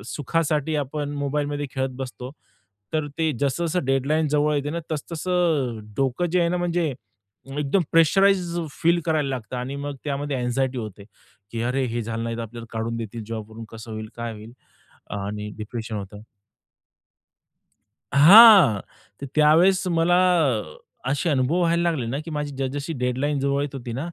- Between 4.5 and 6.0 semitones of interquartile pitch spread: Yes, average, 5.2 semitones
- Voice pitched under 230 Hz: Yes, medium, 140 Hz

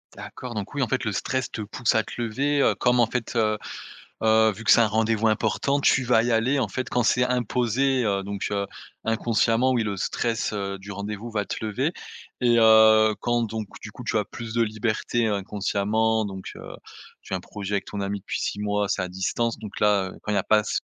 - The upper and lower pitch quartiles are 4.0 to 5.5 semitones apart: No, narrow, 2.6 semitones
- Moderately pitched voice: No, low, 110 Hz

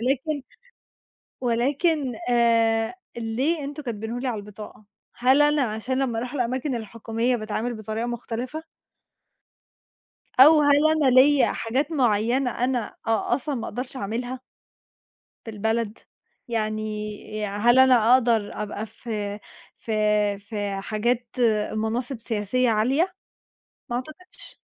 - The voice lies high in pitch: Yes, high, 240 Hz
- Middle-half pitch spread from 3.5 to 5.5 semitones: No, average, 3.0 semitones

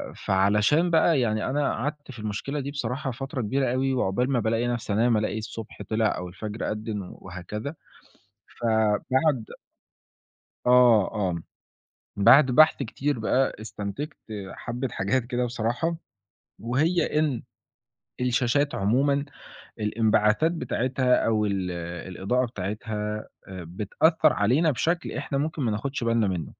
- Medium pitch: No, low, 120 Hz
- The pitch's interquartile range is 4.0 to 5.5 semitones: Yes, average, 4.5 semitones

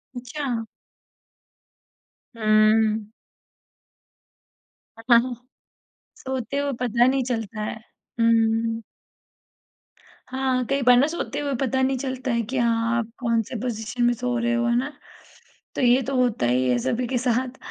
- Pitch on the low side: No, high, 240 Hz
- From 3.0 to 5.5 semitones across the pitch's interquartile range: No, narrow, 2.4 semitones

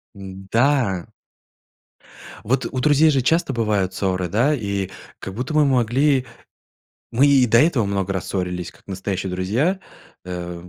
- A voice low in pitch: Yes, low, 110 Hz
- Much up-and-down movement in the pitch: Yes, wide, 6.1 semitones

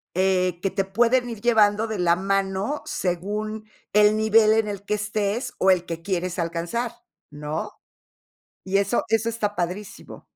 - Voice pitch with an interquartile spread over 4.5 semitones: No, average, 3.0 semitones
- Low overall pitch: No, high, 205 Hz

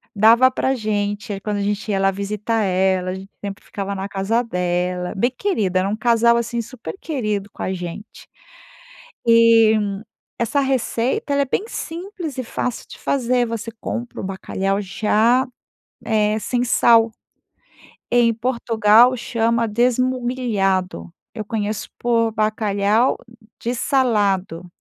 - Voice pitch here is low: No, high, 220 Hz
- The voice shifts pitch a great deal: No, average, 3.4 semitones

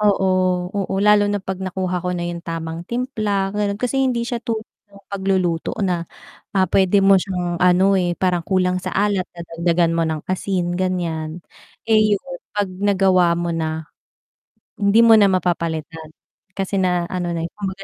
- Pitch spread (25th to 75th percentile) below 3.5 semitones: Yes, narrow, 2.6 semitones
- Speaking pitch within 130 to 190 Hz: Yes, medium, 185 Hz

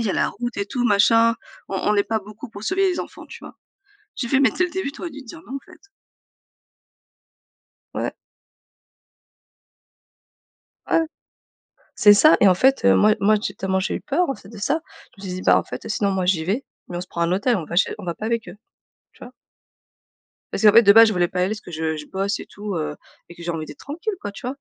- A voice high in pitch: Yes, high, 210 Hz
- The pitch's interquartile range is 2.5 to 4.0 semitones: No, average, 5.0 semitones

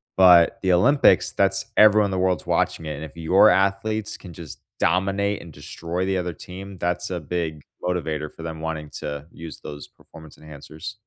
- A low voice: Yes, very low, 90 Hz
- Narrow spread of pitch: No, average, 3.4 semitones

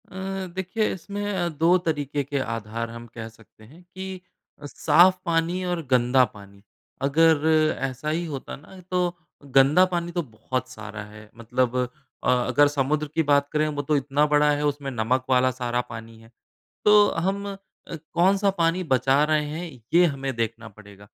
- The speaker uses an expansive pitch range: Yes, wide, 5.7 semitones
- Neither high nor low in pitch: Yes, medium, 145 Hz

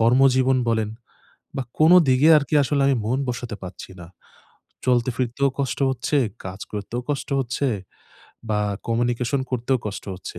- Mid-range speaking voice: No, low, 125 Hz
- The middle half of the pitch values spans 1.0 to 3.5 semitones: Yes, average, 2.8 semitones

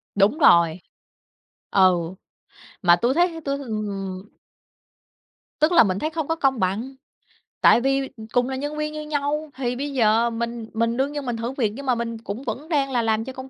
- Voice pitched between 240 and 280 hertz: Yes, very high, 250 Hz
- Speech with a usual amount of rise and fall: Yes, average, 4.3 semitones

